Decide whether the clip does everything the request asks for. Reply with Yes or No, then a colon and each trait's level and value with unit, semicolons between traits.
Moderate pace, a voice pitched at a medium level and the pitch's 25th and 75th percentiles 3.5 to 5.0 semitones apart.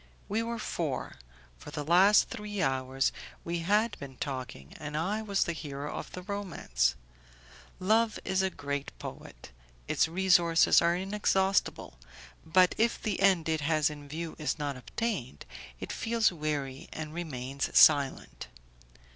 No: average, 145 wpm; medium, 165 Hz; wide, 5.5 semitones